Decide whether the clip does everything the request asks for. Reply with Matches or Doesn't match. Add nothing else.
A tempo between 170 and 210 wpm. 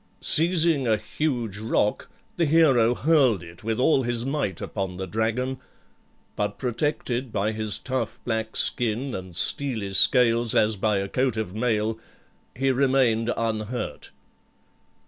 Doesn't match